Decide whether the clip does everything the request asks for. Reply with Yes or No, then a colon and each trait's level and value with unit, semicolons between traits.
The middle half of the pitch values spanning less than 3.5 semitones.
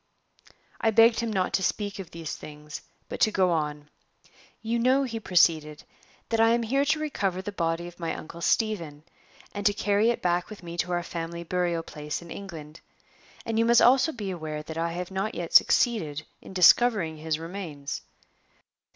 No: average, 5.2 semitones